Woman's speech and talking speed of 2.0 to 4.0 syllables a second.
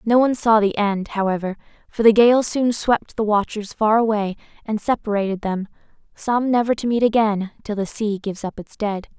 No: female; 5.2 syllables/s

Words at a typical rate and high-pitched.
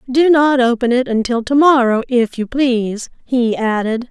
Yes: average, 175 wpm; very high, 250 Hz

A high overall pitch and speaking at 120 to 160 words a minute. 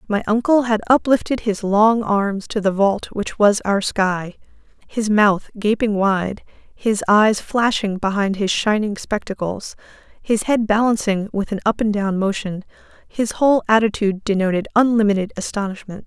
Yes: high, 210 Hz; average, 150 wpm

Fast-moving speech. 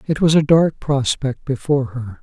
No: average, 190 wpm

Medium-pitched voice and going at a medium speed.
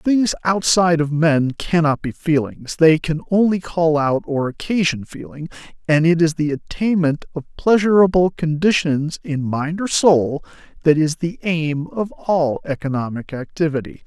Yes: medium, 160 Hz; average, 150 wpm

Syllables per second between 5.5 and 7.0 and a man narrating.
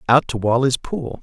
No: 4.8 syllables/s; male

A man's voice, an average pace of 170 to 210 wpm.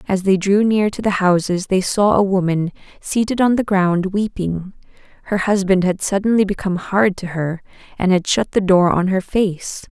No: female; average, 195 wpm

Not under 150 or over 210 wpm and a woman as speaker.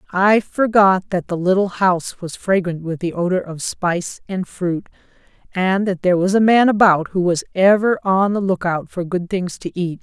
Yes: average, 200 wpm; female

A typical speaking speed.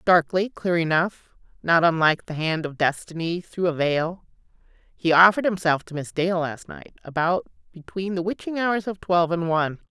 Yes: average, 170 wpm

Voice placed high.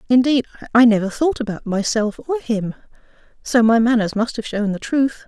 Yes: high, 230 Hz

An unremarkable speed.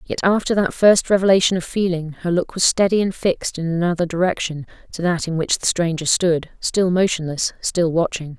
Yes: average, 180 wpm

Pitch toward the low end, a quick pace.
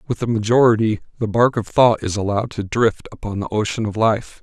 Yes: low, 110 Hz; fast, 215 wpm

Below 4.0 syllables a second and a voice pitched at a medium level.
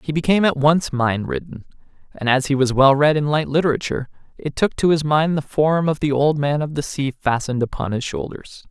No: 5.6 syllables/s; medium, 145 Hz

